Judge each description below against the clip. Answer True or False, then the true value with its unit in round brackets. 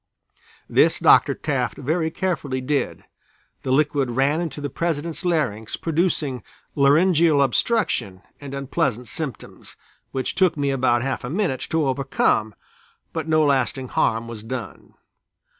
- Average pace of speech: False (130 wpm)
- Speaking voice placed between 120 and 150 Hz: True (140 Hz)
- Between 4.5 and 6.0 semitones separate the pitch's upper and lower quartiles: False (3.8 semitones)